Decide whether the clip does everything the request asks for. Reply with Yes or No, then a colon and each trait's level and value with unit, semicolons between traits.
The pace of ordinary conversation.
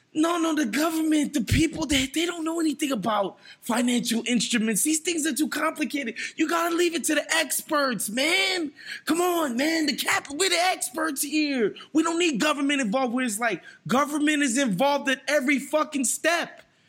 Yes: average, 180 wpm